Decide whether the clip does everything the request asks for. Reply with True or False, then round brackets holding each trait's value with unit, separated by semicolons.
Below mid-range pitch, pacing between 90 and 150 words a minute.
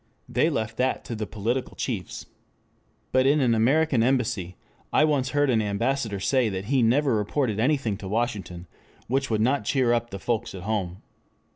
False (115 Hz; 175 wpm)